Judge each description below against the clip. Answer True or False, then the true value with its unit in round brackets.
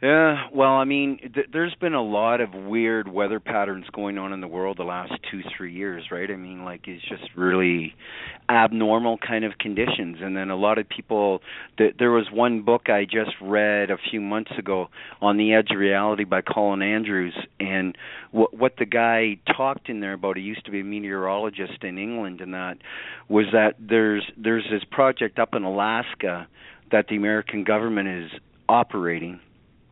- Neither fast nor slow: True (185 wpm)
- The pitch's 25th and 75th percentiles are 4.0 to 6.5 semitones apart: False (2.8 semitones)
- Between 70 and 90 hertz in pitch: False (105 Hz)